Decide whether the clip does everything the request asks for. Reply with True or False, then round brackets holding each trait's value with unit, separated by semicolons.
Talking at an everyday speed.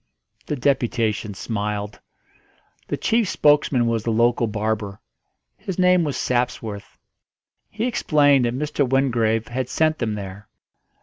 False (125 wpm)